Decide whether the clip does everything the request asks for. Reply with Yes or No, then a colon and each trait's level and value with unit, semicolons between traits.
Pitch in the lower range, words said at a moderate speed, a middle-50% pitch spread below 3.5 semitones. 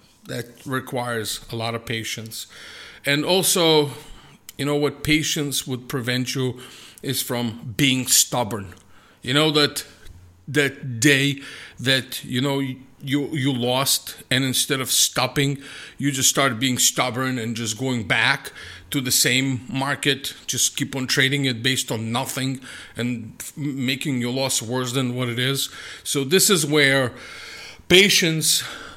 Yes: low, 130 Hz; average, 145 wpm; narrow, 2.5 semitones